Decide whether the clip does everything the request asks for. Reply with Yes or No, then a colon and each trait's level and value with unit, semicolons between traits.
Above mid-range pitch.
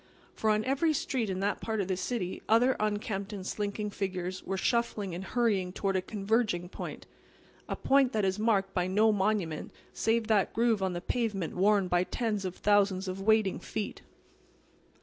Yes: high, 205 Hz